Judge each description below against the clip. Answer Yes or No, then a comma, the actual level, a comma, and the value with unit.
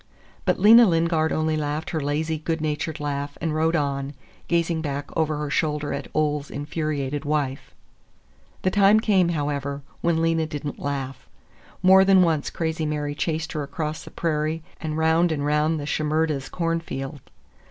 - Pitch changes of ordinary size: No, narrow, 2.0 semitones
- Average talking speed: Yes, average, 165 wpm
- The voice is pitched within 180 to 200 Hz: No, medium, 155 Hz